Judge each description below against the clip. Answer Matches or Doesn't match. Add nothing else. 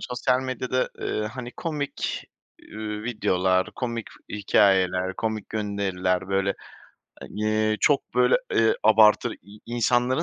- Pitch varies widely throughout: Doesn't match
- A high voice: Doesn't match